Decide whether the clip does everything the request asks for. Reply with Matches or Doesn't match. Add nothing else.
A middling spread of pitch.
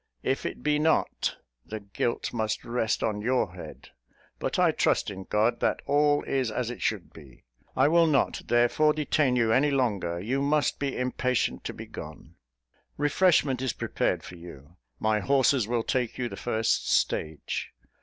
Matches